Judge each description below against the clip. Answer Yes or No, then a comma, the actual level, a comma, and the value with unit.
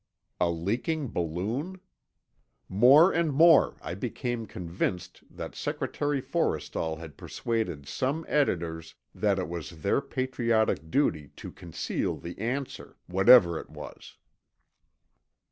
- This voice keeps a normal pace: No, slow, 110 wpm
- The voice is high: No, low, 110 Hz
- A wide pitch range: Yes, wide, 7.9 semitones